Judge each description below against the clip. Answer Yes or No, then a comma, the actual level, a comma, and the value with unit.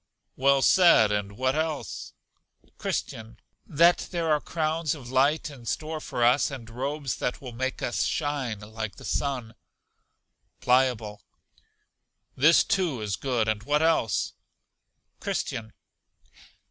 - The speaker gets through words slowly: Yes, slow, 125 wpm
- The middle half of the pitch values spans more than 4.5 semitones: Yes, average, 5.0 semitones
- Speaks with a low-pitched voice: Yes, low, 130 Hz